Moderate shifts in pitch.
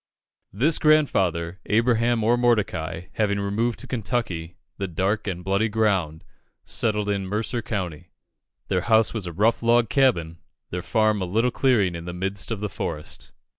Yes: average, 4.4 semitones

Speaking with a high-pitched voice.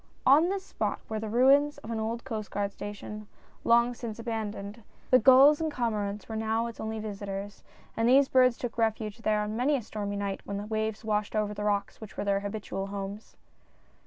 Yes: high, 220 Hz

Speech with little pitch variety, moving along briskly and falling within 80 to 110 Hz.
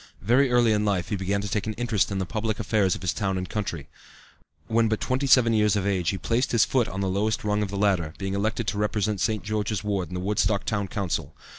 Yes: narrow, 2.3 semitones; fast, 255 wpm; low, 105 Hz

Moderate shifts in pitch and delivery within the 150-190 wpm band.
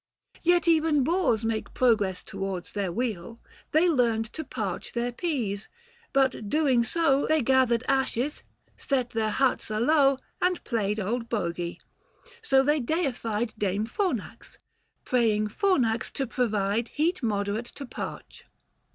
No: average, 4.9 semitones; slow, 135 wpm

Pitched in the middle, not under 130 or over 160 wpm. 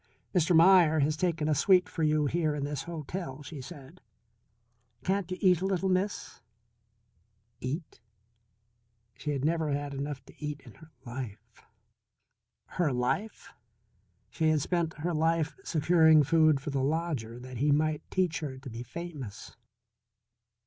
Yes: medium, 155 Hz; average, 150 wpm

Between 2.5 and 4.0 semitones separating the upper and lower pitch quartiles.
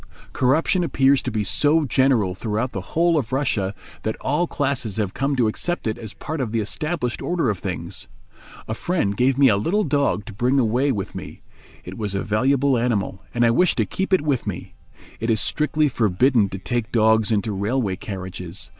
No: average, 5.2 semitones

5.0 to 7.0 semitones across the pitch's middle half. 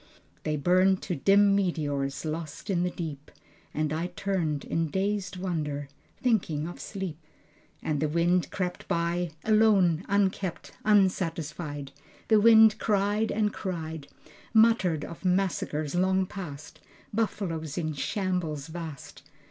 No: average, 4.0 semitones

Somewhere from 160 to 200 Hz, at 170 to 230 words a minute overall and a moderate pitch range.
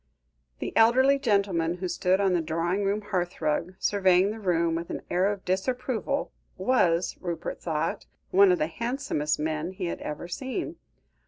No: medium, 185 Hz; average, 160 wpm; average, 3.8 semitones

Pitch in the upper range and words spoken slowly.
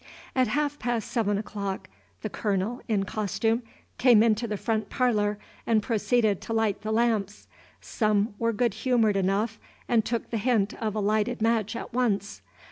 No: high, 220 Hz; average, 165 wpm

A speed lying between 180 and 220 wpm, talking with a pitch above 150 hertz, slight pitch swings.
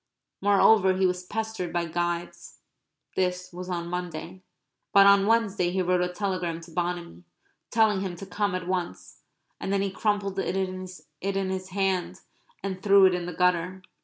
No: average, 165 wpm; medium, 185 Hz; narrow, 1.8 semitones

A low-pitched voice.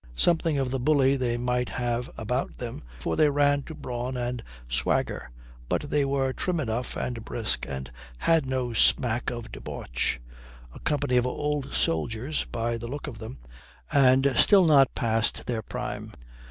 Yes: low, 125 Hz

